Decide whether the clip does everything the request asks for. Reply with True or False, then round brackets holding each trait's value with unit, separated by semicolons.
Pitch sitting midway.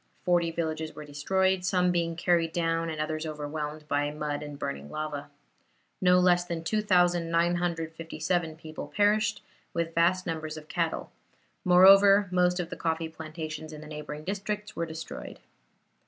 True (165 Hz)